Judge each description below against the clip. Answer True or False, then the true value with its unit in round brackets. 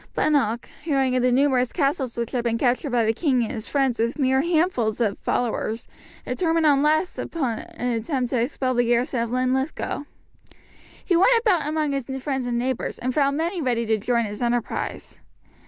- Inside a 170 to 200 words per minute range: True (190 wpm)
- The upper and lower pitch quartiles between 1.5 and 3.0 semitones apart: False (3.7 semitones)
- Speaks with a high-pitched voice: True (255 Hz)